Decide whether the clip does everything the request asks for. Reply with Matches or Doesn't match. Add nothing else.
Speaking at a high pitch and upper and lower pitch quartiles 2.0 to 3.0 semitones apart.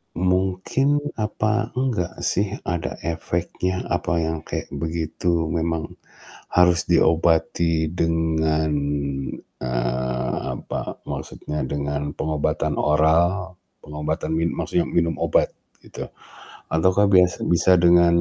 Doesn't match